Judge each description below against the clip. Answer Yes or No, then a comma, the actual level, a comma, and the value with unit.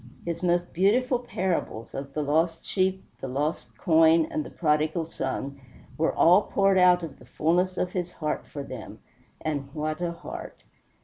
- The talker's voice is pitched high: No, medium, 165 Hz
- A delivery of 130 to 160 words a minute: No, average, 170 wpm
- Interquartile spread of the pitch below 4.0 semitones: Yes, average, 3.1 semitones